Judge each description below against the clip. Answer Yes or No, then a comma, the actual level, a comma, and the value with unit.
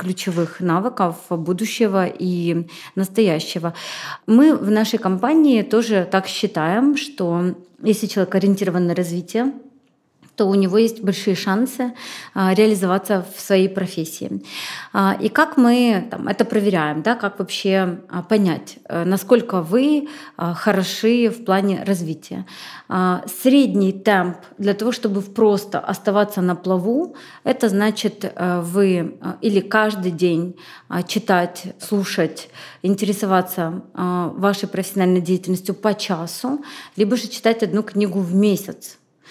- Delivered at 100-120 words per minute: Yes, average, 115 wpm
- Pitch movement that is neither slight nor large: Yes, average, 3.3 semitones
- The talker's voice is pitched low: No, high, 195 Hz